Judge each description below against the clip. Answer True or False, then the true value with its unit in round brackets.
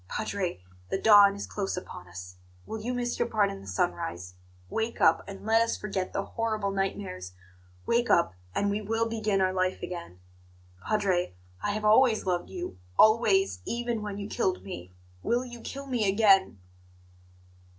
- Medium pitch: False (200 Hz)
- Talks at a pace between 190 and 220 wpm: False (170 wpm)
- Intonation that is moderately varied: True (3.6 semitones)